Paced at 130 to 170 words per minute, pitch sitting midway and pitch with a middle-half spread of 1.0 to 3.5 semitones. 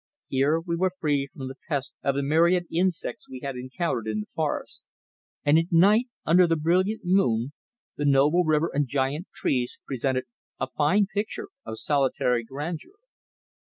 No: average, 160 wpm; medium, 150 Hz; average, 4.8 semitones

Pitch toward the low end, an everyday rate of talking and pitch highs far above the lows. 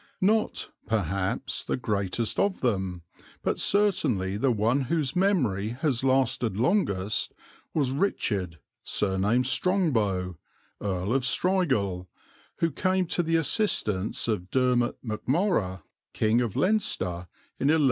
No: low, 120 Hz; slow, 115 wpm; wide, 8.2 semitones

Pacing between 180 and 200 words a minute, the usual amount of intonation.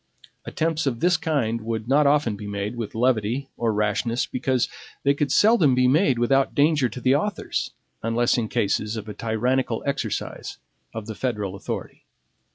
No: average, 165 wpm; average, 4.1 semitones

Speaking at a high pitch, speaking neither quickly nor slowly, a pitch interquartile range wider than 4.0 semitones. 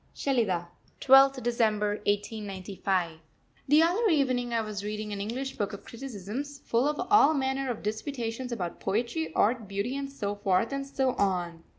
Yes: high, 230 Hz; average, 160 wpm; average, 5.0 semitones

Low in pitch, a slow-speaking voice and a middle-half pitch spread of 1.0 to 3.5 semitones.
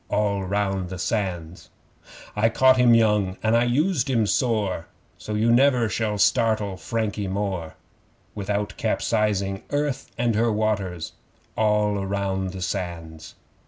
Yes: low, 105 Hz; slow, 130 wpm; average, 3.0 semitones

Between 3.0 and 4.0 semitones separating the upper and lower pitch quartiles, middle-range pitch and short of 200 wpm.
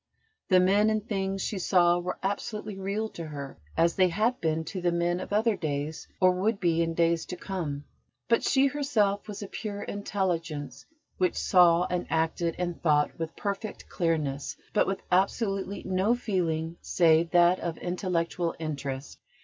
Yes: average, 3.3 semitones; medium, 180 Hz; average, 165 wpm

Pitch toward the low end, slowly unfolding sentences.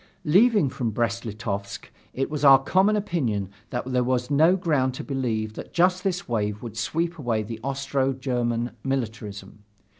No: low, 130 Hz; average, 160 wpm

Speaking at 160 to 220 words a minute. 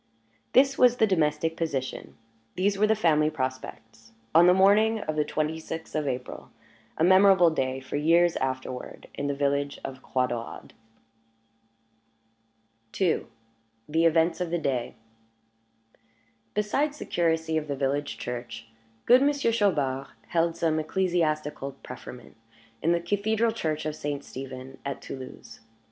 No: average, 140 wpm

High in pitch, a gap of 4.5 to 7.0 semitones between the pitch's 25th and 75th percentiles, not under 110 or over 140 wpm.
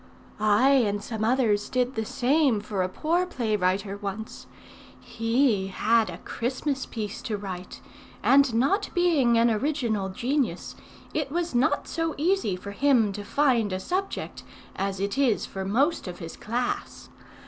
No: high, 230 Hz; wide, 5.5 semitones; average, 155 wpm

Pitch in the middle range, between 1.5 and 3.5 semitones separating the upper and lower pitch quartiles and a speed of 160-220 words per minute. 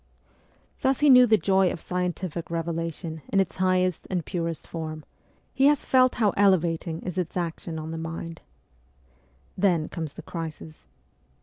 No: medium, 170 Hz; average, 2.7 semitones; average, 150 wpm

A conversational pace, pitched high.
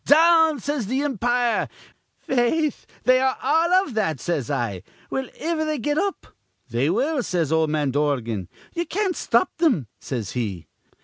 Yes: average, 160 wpm; high, 245 Hz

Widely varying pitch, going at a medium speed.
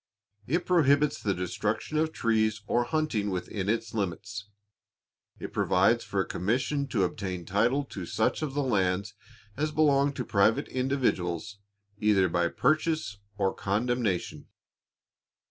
No: wide, 6.0 semitones; slow, 130 wpm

